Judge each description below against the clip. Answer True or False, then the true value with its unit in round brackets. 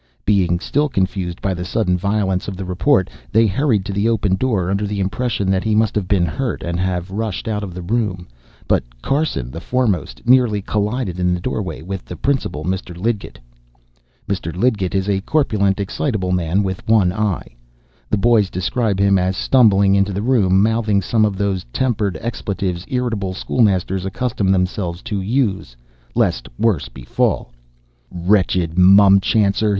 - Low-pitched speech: True (100 Hz)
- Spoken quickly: False (165 wpm)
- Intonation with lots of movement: False (3.0 semitones)